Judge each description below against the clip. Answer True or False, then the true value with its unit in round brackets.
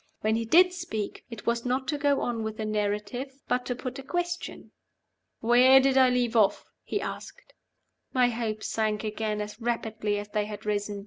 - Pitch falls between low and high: False (230 Hz)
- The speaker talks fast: False (190 wpm)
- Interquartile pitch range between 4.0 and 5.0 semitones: False (3.5 semitones)